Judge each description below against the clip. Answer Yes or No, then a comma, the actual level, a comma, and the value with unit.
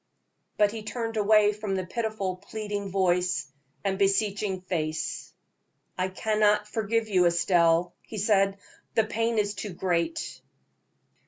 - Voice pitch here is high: Yes, high, 200 Hz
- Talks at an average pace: No, slow, 130 wpm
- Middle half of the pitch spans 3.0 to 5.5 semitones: No, narrow, 2.6 semitones